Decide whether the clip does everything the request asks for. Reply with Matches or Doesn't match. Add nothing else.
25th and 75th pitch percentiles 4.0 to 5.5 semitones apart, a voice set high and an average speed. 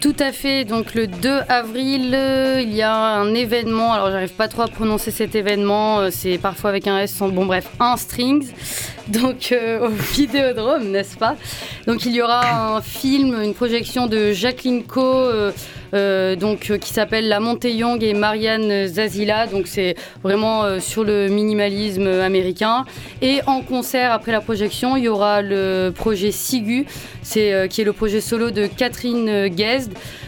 Doesn't match